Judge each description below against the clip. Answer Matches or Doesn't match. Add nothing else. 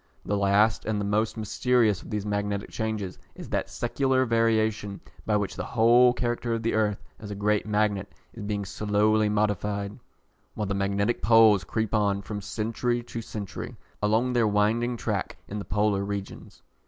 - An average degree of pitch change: Doesn't match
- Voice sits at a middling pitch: Doesn't match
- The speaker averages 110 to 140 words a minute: Doesn't match